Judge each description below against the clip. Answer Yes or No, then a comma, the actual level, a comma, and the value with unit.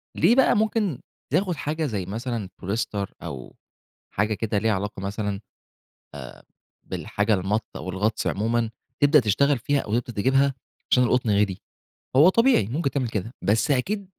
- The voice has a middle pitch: No, low, 115 Hz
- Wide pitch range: Yes, wide, 5.7 semitones